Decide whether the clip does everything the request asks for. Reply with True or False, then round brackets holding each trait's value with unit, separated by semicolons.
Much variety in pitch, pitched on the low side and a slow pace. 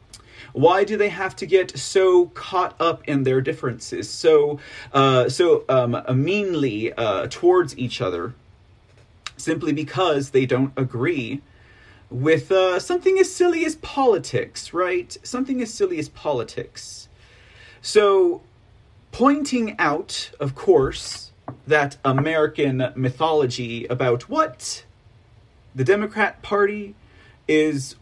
False (8.7 semitones; 150 Hz; 115 wpm)